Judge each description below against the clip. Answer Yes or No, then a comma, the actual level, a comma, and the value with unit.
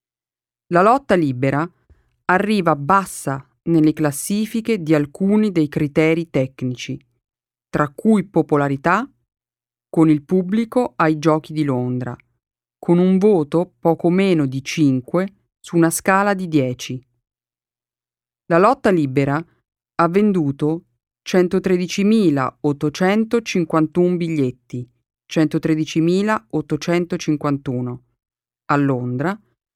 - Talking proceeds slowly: Yes, slow, 90 wpm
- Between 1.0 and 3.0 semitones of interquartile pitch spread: No, average, 5.1 semitones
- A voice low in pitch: No, medium, 160 Hz